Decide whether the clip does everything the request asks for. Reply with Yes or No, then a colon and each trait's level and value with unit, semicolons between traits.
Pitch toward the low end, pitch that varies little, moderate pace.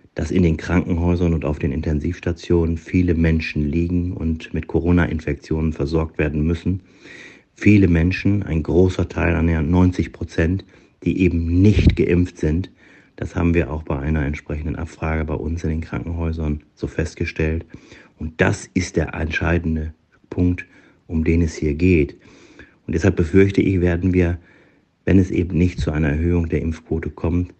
Yes: very low, 85 Hz; narrow, 1.9 semitones; average, 155 wpm